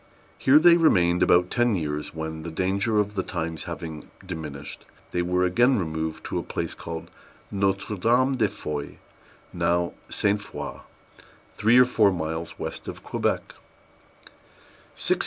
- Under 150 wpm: Yes, average, 140 wpm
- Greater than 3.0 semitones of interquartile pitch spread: Yes, average, 4.6 semitones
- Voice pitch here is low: Yes, very low, 90 Hz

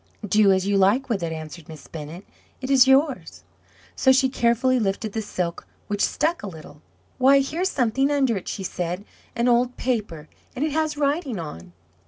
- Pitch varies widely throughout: Yes, wide, 6.5 semitones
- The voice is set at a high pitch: Yes, high, 230 Hz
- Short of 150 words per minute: No, average, 185 wpm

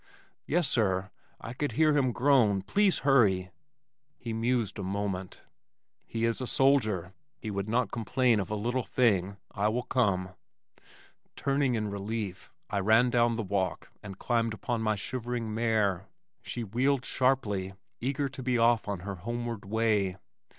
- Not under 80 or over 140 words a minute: No, average, 155 wpm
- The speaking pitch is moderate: No, low, 115 Hz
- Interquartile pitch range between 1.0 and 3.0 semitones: No, average, 3.8 semitones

